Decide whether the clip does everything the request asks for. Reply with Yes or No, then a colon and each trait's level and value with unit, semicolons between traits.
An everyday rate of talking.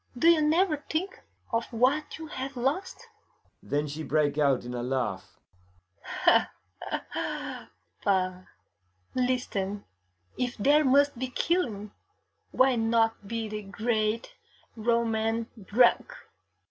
No: slow, 110 wpm